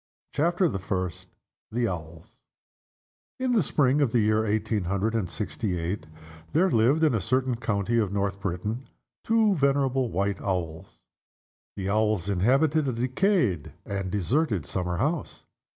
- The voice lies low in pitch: Yes, low, 110 Hz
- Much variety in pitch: Yes, wide, 6.2 semitones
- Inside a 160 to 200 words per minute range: No, average, 145 wpm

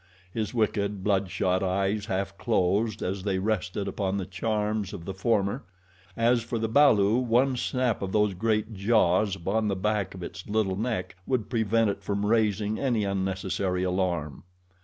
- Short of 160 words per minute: No, average, 165 wpm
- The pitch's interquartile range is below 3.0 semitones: Yes, narrow, 2.6 semitones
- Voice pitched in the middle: No, low, 100 Hz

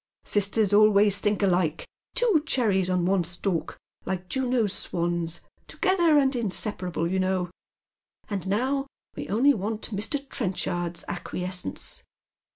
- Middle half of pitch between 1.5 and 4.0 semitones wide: No, average, 4.9 semitones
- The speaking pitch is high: Yes, high, 200 Hz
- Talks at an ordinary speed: No, slow, 125 wpm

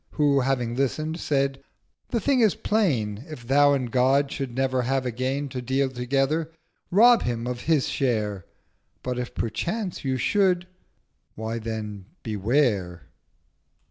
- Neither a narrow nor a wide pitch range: Yes, average, 3.9 semitones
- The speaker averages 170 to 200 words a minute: No, slow, 135 wpm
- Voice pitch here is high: No, low, 135 Hz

